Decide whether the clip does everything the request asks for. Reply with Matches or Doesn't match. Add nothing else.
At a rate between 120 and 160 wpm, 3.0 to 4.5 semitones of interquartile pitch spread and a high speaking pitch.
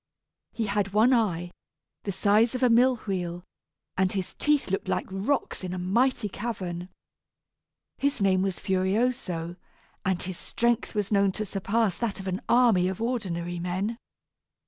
Matches